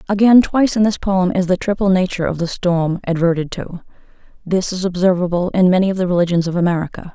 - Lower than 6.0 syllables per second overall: No, 6.4 syllables/s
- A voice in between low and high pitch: Yes, medium, 180 Hz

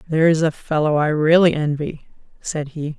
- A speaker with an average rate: Yes, average, 160 wpm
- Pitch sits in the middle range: Yes, medium, 155 Hz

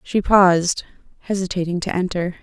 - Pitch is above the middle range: No, medium, 180 Hz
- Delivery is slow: Yes, slow, 125 wpm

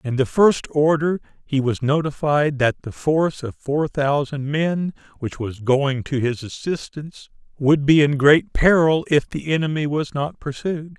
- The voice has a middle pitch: Yes, medium, 145 Hz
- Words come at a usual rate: Yes, average, 170 wpm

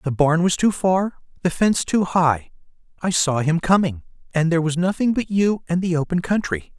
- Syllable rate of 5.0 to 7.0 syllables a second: Yes, 5.2 syllables/s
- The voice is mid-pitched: Yes, medium, 170 Hz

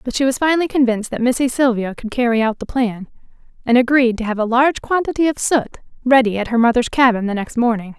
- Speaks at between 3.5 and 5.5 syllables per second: No, 6.4 syllables/s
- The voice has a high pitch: Yes, high, 245 Hz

